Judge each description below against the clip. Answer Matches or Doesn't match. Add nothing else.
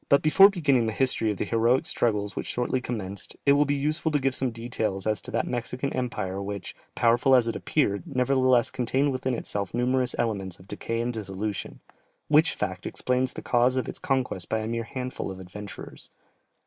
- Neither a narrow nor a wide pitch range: Matches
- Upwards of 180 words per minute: Matches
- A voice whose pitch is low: Matches